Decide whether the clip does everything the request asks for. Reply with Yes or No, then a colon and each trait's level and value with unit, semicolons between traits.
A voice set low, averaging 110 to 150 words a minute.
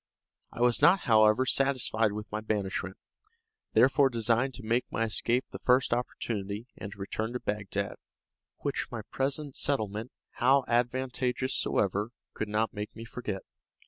Yes: low, 115 Hz; average, 145 wpm